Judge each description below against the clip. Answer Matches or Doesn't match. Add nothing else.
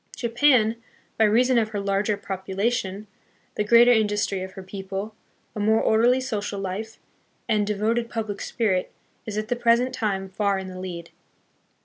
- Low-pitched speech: Doesn't match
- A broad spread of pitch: Doesn't match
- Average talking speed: Matches